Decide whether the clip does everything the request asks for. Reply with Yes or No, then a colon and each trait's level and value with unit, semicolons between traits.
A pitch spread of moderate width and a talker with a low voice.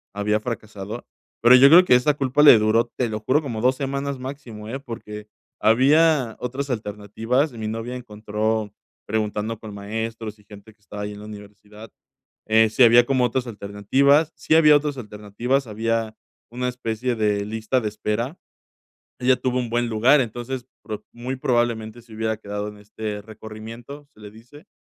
Yes: average, 3.1 semitones; low, 115 Hz